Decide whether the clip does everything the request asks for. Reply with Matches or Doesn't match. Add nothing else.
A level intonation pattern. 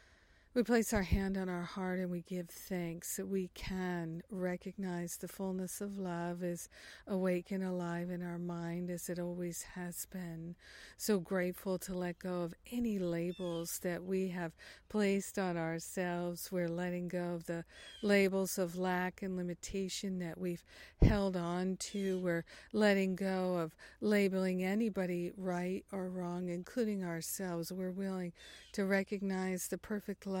Matches